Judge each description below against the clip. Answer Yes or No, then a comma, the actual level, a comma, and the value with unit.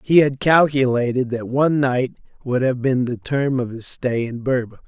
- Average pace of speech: Yes, average, 195 wpm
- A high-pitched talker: No, low, 130 Hz